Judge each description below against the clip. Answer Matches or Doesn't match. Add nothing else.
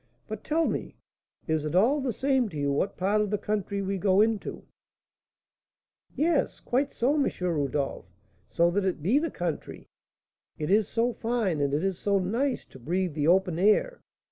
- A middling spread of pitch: Doesn't match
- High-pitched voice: Matches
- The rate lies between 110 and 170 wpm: Doesn't match